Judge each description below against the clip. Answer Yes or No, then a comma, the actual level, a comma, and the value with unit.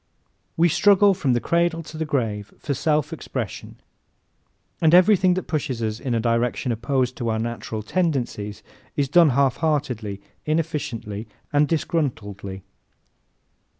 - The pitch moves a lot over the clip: Yes, wide, 6.1 semitones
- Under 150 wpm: Yes, slow, 135 wpm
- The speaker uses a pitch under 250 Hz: Yes, low, 135 Hz